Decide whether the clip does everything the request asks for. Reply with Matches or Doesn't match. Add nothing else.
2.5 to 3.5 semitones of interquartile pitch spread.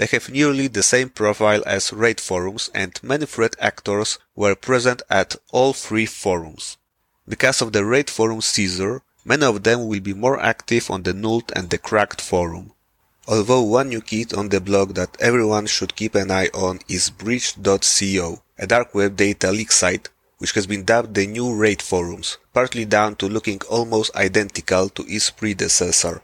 Matches